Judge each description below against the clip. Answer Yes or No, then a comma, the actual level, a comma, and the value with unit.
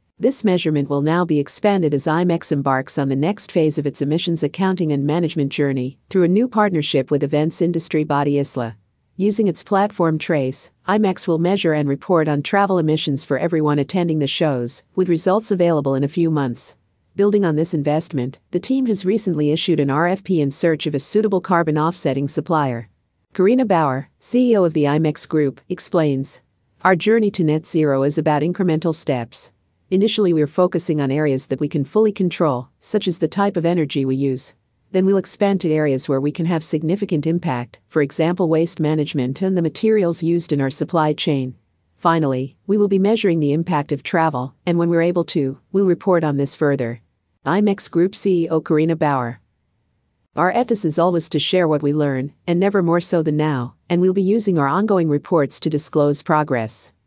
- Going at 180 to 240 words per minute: Yes, average, 190 wpm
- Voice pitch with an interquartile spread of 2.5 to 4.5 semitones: Yes, average, 4.0 semitones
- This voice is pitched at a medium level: Yes, medium, 160 Hz